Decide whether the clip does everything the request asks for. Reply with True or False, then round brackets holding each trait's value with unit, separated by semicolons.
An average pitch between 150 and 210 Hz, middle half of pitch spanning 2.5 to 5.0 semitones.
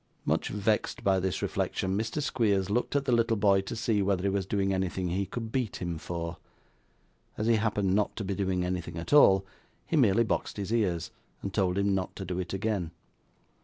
False (100 Hz; 2.8 semitones)